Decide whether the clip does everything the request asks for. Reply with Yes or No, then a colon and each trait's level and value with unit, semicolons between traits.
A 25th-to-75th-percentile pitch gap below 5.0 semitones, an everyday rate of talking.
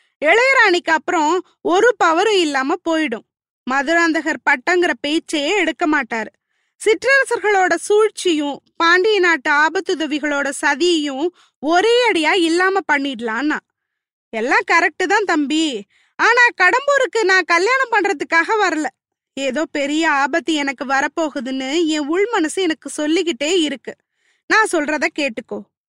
Yes: average, 4.3 semitones; average, 100 wpm